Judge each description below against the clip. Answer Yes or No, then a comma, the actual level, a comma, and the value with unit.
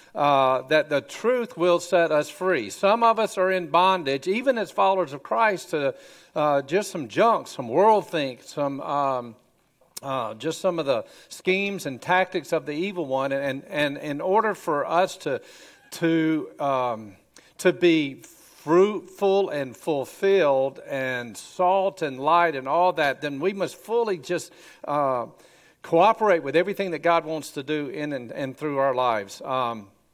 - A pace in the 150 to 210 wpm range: Yes, average, 165 wpm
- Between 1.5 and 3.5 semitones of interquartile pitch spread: No, average, 5.2 semitones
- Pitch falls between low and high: Yes, medium, 160 Hz